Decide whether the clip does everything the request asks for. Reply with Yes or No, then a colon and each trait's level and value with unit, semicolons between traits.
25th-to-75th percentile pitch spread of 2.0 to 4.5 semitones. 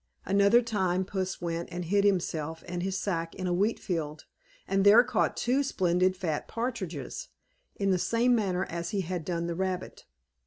Yes: average, 2.8 semitones